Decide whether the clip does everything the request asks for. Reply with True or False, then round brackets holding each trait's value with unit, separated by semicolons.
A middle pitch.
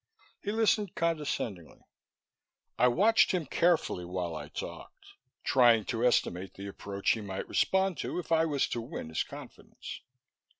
False (125 Hz)